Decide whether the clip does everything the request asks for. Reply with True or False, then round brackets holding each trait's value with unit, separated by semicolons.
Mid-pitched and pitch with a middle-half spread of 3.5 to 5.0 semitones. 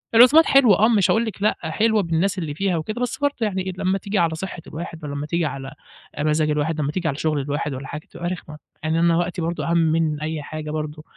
True (165 Hz; 4.3 semitones)